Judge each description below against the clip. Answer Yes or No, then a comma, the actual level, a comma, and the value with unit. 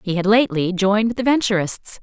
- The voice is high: Yes, high, 205 Hz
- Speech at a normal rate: Yes, average, 180 wpm